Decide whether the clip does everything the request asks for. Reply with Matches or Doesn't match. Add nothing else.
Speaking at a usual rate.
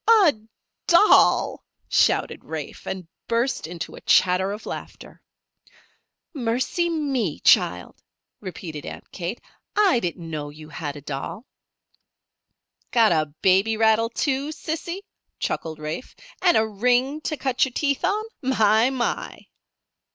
Doesn't match